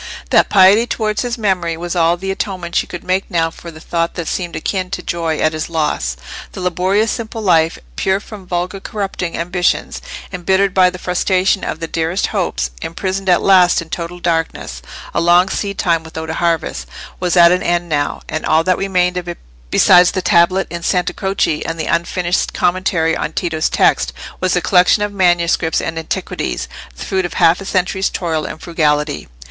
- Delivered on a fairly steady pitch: Yes, narrow, 2.3 semitones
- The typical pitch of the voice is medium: Yes, medium, 175 Hz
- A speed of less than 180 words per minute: No, average, 185 wpm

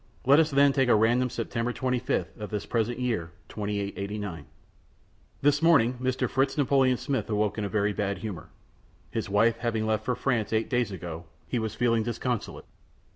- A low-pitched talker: Yes, low, 115 Hz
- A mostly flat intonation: No, average, 3.5 semitones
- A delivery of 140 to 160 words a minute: No, average, 170 wpm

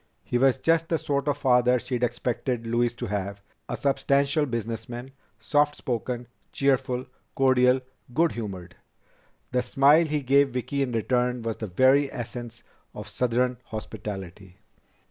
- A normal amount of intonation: Yes, average, 3.1 semitones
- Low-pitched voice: Yes, low, 125 Hz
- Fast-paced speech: No, average, 140 wpm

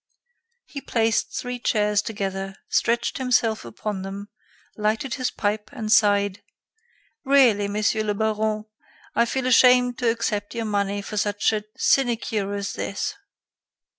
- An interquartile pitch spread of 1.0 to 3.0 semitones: Yes, narrow, 2.6 semitones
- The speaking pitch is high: Yes, high, 215 Hz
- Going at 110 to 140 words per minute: Yes, slow, 135 wpm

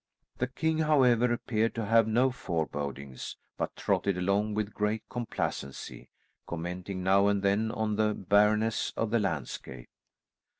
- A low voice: Yes, low, 105 Hz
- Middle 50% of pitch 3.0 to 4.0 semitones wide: Yes, average, 3.4 semitones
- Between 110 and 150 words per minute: Yes, slow, 135 wpm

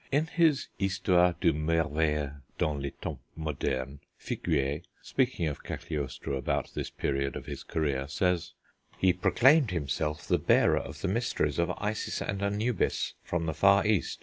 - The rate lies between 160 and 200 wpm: No, average, 150 wpm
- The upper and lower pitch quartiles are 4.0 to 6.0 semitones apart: Yes, average, 5.2 semitones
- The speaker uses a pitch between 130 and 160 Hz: No, very low, 85 Hz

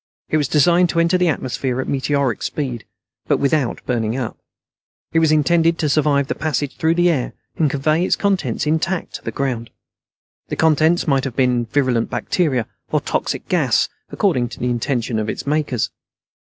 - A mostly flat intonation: No, average, 4.3 semitones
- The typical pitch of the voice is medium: Yes, medium, 145 Hz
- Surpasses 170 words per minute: Yes, average, 180 wpm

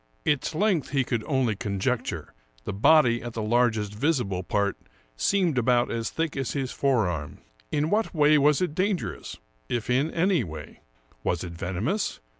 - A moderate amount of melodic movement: No, wide, 6.5 semitones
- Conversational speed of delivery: Yes, average, 165 wpm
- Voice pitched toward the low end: Yes, low, 125 Hz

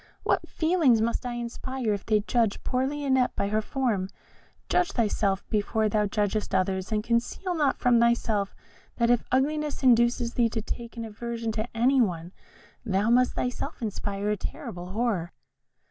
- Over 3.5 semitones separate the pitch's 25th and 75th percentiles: No, average, 3.2 semitones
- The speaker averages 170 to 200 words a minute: No, average, 160 wpm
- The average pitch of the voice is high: Yes, high, 230 Hz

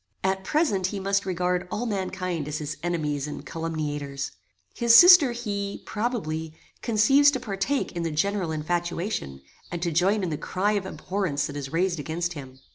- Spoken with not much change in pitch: No, average, 4.5 semitones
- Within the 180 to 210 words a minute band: No, average, 170 wpm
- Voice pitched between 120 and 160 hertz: No, medium, 180 Hz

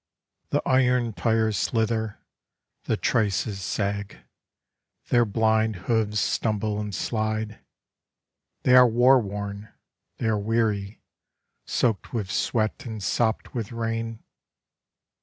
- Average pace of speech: No, slow, 105 wpm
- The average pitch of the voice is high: No, low, 110 Hz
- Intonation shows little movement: Yes, narrow, 1.8 semitones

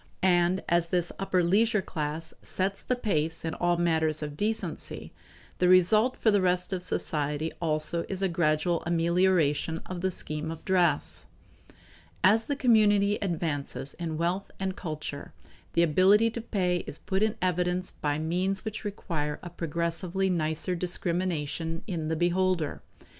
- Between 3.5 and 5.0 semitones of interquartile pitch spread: No, average, 2.8 semitones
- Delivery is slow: No, average, 150 wpm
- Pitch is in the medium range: Yes, medium, 175 Hz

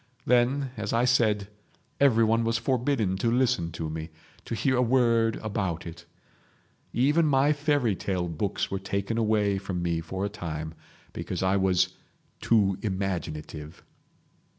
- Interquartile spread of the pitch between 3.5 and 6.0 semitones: Yes, average, 4.7 semitones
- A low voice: Yes, low, 105 Hz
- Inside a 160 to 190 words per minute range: No, average, 140 wpm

